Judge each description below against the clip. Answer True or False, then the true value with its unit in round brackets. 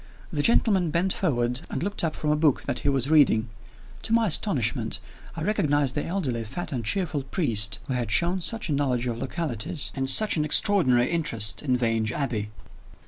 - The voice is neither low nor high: True (145 Hz)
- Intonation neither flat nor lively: False (5.9 semitones)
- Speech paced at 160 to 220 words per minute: True (190 wpm)